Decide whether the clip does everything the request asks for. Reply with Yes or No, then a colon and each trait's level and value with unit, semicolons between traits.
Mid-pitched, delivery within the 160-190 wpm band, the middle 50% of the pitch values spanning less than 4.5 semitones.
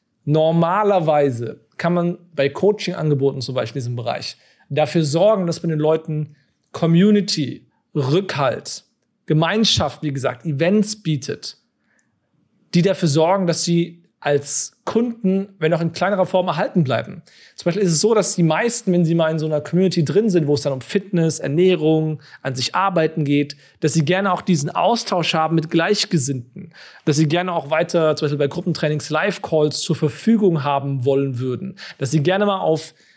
Yes: medium, 165 Hz; average, 170 wpm; average, 3.6 semitones